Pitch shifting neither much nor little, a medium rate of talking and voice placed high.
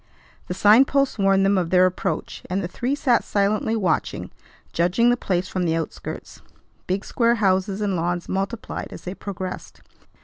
Yes: average, 3.2 semitones; average, 170 wpm; high, 195 Hz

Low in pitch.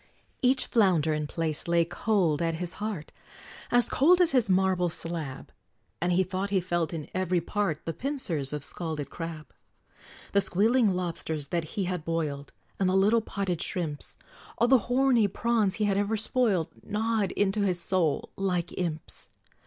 No: medium, 185 Hz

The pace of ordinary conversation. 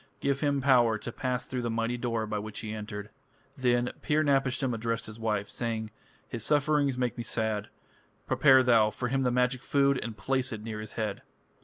Yes: average, 195 wpm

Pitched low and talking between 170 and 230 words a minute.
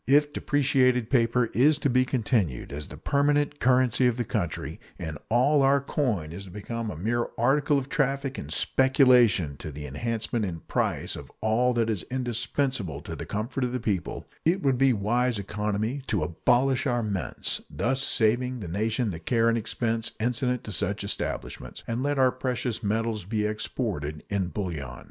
Yes: low, 115 Hz; average, 175 wpm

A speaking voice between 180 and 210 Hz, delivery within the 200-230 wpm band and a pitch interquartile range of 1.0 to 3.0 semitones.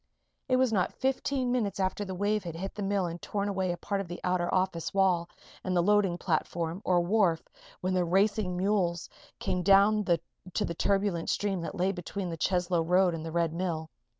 Yes: medium, 185 Hz; fast, 205 wpm; narrow, 2.6 semitones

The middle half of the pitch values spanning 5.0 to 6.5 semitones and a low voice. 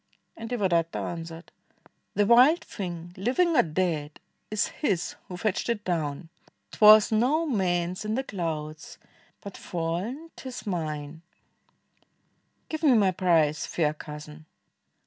No: wide, 5.5 semitones; medium, 180 Hz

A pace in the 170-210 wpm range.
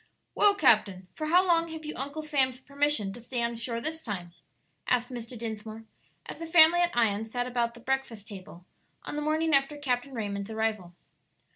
Yes: average, 190 wpm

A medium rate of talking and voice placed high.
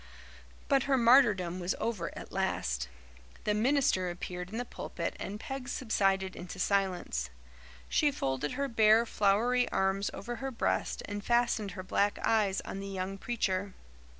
Yes: average, 150 wpm; high, 205 Hz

